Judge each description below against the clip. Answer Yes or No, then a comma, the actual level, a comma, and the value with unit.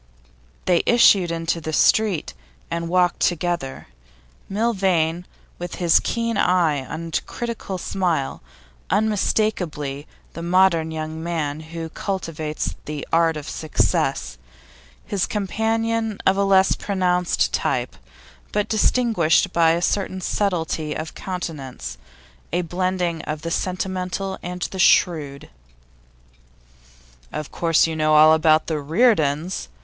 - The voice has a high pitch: No, medium, 170 Hz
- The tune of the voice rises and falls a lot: No, average, 3.3 semitones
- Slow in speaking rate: Yes, slow, 120 wpm